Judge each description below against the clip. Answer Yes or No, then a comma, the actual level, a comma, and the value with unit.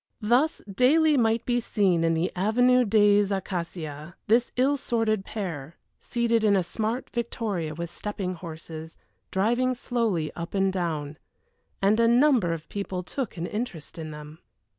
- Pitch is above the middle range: Yes, high, 200 Hz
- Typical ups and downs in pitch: No, wide, 5.8 semitones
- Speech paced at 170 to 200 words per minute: No, average, 150 wpm